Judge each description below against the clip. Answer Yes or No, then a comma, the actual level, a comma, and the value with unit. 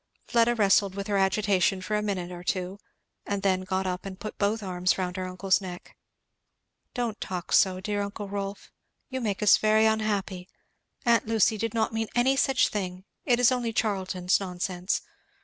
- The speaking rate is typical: Yes, average, 180 wpm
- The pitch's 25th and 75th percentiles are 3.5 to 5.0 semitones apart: No, average, 2.8 semitones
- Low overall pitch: No, high, 200 Hz